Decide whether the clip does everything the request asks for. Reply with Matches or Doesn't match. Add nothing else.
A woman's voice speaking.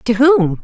Matches